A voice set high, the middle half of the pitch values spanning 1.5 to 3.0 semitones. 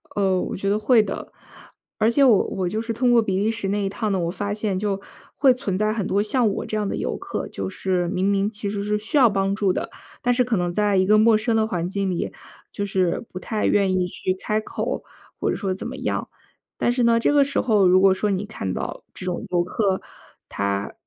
Yes: high, 200 Hz; average, 2.7 semitones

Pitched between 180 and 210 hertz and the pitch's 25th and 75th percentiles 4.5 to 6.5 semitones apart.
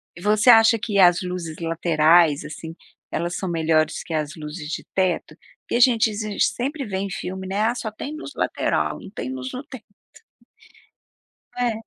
Yes: medium, 185 Hz; wide, 5.4 semitones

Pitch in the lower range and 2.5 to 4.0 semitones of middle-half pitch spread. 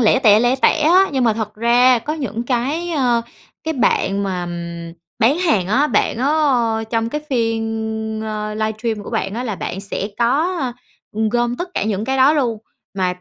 No: high, 235 Hz; average, 3.6 semitones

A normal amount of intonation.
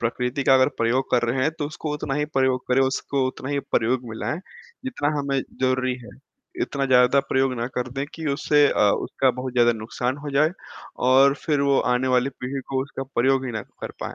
No: narrow, 1.8 semitones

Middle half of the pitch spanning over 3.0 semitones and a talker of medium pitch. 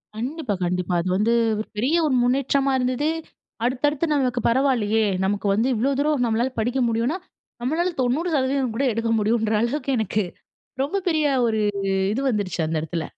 No: average, 4.2 semitones; high, 245 Hz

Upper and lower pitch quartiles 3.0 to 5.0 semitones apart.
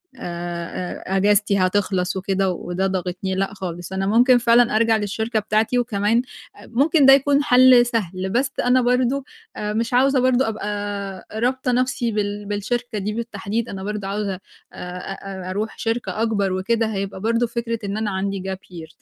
Yes: average, 3.7 semitones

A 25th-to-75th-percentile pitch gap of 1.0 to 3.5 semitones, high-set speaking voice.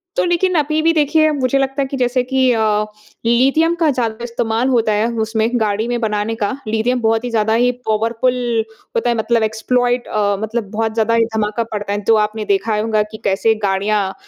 Yes: narrow, 2.6 semitones; high, 230 Hz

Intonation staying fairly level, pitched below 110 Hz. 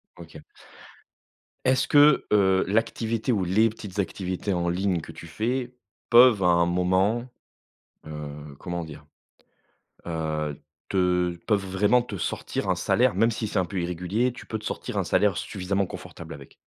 No: average, 4.2 semitones; very low, 95 Hz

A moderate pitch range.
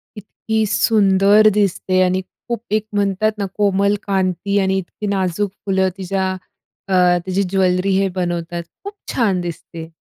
No: narrow, 1.7 semitones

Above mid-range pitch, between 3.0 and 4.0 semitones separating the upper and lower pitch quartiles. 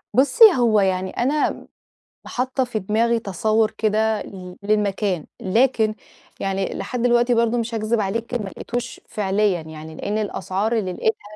Yes: high, 215 Hz; average, 3.4 semitones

